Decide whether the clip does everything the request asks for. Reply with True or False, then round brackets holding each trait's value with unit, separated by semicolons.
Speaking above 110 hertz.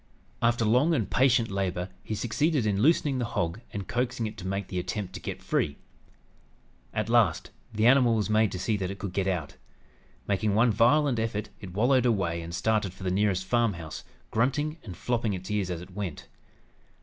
False (105 Hz)